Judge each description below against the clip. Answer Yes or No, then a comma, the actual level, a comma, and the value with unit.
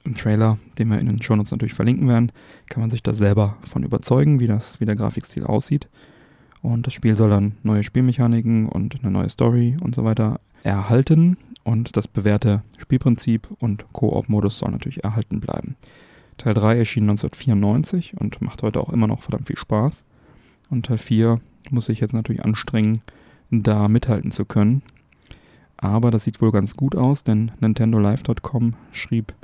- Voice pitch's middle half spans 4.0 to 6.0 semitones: No, narrow, 2.6 semitones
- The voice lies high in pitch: No, low, 115 Hz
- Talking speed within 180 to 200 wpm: No, average, 170 wpm